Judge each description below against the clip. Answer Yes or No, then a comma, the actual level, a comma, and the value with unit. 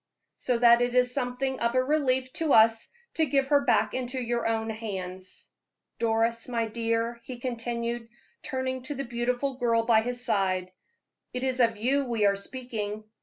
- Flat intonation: Yes, narrow, 2.2 semitones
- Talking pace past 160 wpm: Yes, average, 170 wpm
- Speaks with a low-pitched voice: No, high, 240 Hz